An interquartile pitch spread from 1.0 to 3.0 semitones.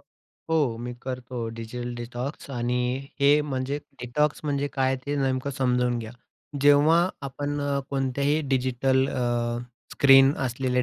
Yes: narrow, 2.4 semitones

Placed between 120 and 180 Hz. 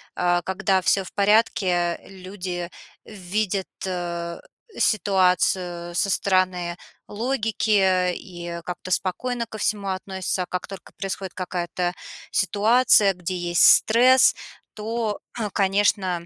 No: high, 190 Hz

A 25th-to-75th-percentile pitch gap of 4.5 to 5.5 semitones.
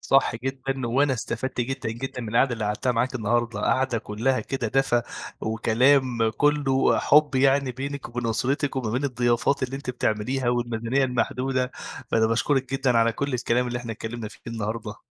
No: narrow, 2.5 semitones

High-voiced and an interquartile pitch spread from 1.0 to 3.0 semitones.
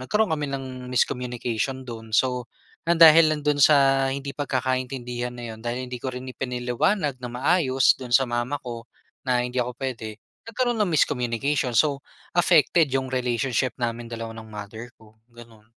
No: low, 125 Hz; narrow, 2.6 semitones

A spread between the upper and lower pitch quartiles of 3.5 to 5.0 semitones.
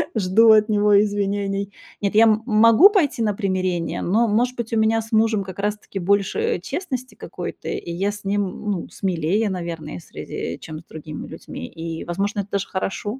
No: average, 2.8 semitones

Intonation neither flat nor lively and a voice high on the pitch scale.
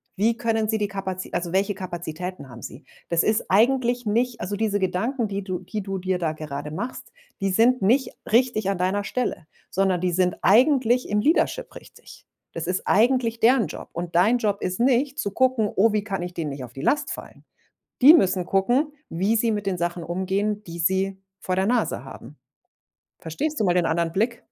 Yes: average, 4.4 semitones; high, 195 Hz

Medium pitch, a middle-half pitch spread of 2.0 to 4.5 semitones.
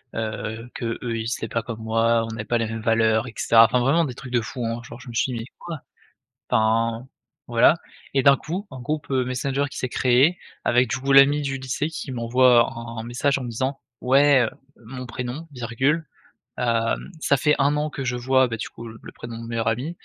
No: low, 125 Hz; average, 2.8 semitones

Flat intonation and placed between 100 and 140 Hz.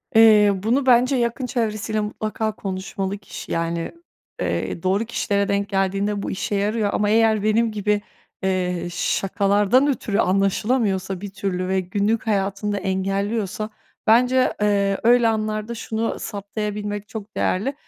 No: narrow, 2.1 semitones; high, 205 Hz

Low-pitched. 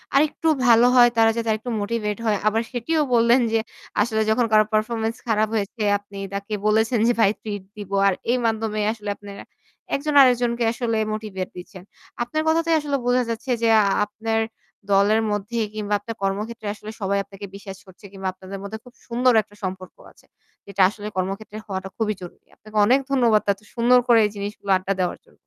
No: high, 220 Hz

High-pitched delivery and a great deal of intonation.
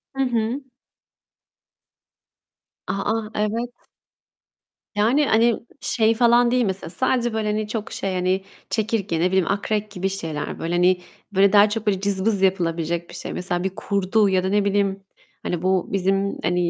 No: high, 200 Hz; average, 2.9 semitones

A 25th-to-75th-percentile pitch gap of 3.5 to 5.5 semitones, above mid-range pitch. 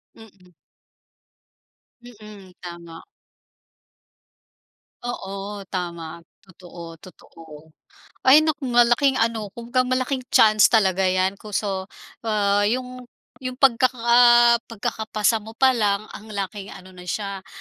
Yes: average, 4.3 semitones; high, 215 Hz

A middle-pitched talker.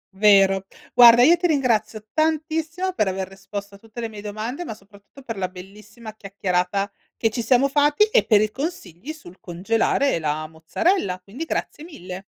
No: high, 215 Hz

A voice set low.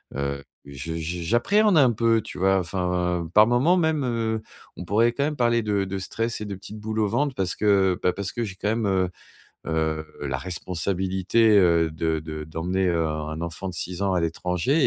Yes: very low, 95 Hz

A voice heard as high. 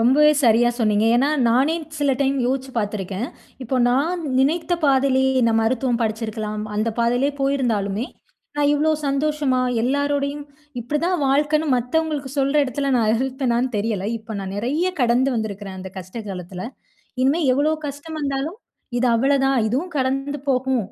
Yes: very high, 260 Hz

